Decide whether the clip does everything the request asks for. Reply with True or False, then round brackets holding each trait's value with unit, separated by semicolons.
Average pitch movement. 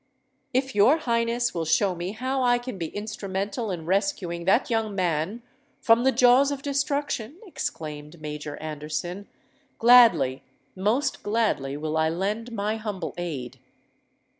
False (6.2 semitones)